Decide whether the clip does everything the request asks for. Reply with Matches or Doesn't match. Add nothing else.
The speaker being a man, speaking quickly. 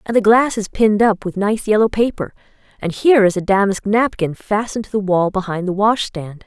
Doesn't match